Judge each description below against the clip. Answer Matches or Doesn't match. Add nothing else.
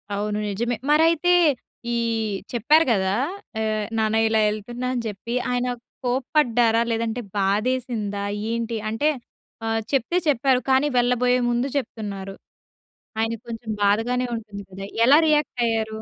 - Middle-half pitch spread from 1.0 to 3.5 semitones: Matches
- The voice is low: Doesn't match